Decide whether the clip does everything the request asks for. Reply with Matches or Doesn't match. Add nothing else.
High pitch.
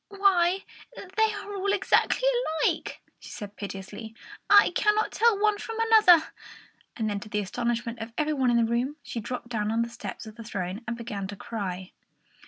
Matches